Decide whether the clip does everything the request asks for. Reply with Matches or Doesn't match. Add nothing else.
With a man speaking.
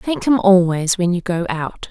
Doesn't match